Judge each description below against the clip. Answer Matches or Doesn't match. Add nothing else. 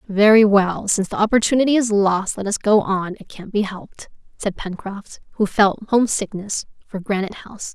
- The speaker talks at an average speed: Matches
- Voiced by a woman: Matches